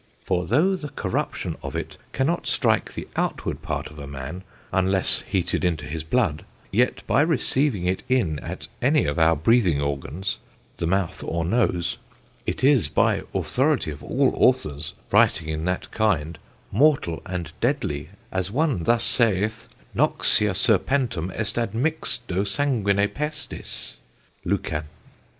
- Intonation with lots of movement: Yes, wide, 7.3 semitones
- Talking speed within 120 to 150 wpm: Yes, average, 140 wpm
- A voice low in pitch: Yes, very low, 95 Hz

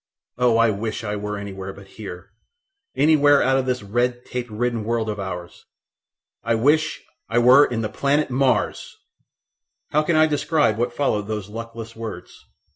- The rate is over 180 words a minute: No, average, 160 wpm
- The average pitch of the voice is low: Yes, low, 115 Hz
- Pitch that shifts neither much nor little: Yes, average, 4.0 semitones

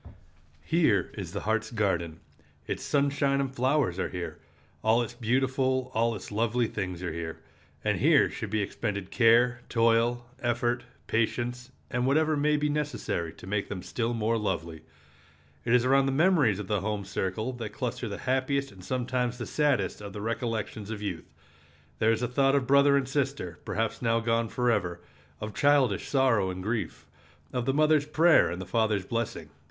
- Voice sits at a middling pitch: No, low, 115 Hz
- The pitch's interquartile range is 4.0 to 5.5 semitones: Yes, average, 4.3 semitones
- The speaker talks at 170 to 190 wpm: Yes, average, 175 wpm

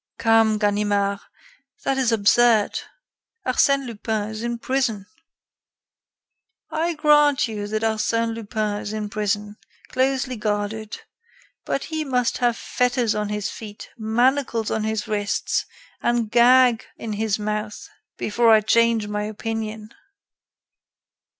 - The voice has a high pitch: Yes, high, 220 Hz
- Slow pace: Yes, slow, 120 wpm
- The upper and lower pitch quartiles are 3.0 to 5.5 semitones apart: No, narrow, 2.4 semitones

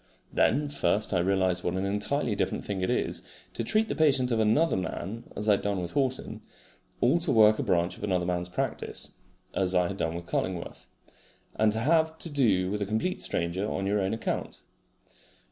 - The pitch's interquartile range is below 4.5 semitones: No, wide, 5.4 semitones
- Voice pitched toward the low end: Yes, low, 105 Hz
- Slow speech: No, average, 200 wpm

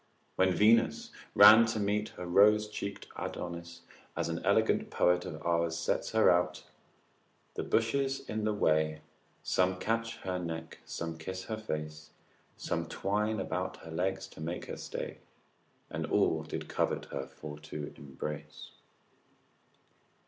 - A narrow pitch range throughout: No, average, 4.6 semitones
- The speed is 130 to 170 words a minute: Yes, average, 140 wpm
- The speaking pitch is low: Yes, very low, 90 Hz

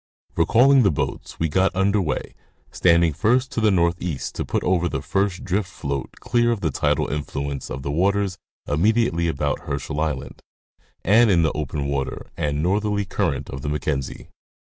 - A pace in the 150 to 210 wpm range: Yes, average, 175 wpm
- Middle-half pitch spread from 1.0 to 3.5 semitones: No, wide, 5.6 semitones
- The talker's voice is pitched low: Yes, very low, 85 Hz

